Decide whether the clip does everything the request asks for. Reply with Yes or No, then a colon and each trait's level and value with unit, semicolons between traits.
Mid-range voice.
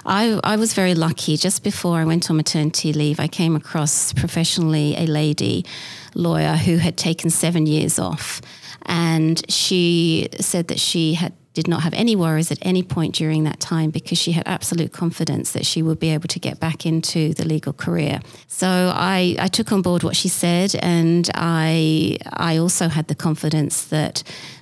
Yes: medium, 165 Hz